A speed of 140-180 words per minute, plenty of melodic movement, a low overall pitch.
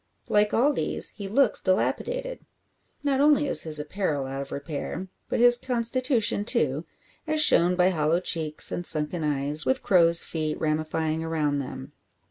No: average, 155 wpm; wide, 7.6 semitones; medium, 170 Hz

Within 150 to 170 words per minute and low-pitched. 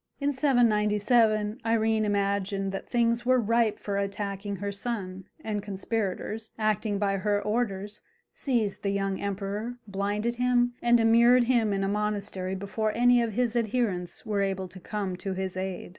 No: average, 160 wpm; high, 210 Hz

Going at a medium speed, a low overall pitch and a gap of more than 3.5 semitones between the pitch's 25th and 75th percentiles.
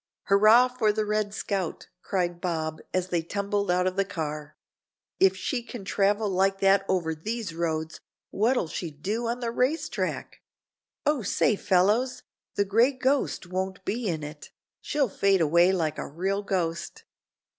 No: average, 160 wpm; high, 195 Hz; average, 4.0 semitones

